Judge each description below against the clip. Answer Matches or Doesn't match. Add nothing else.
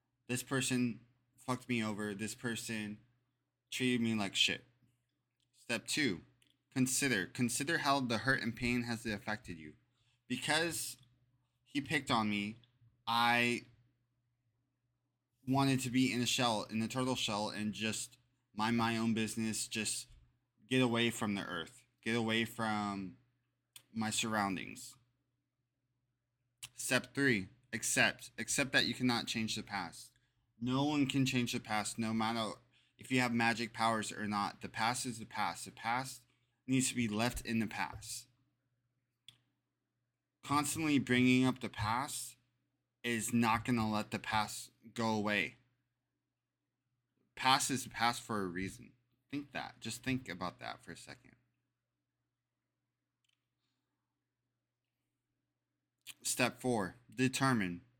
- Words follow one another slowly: Matches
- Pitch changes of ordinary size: Doesn't match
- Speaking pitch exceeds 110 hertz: Matches